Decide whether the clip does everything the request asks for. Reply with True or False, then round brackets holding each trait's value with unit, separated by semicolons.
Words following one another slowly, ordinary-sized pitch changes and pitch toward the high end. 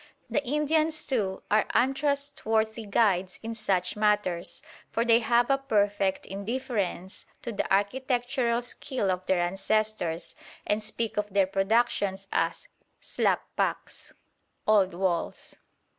True (120 wpm; 4.0 semitones; 215 Hz)